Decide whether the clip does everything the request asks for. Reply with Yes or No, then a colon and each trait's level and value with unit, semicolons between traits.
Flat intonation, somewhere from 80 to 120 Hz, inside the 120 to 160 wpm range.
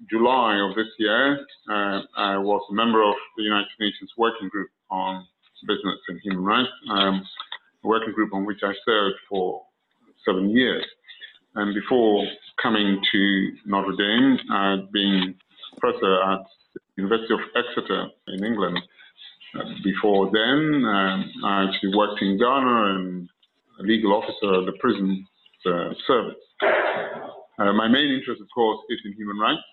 Yes: narrow, 2.2 semitones; low, 100 Hz; average, 145 wpm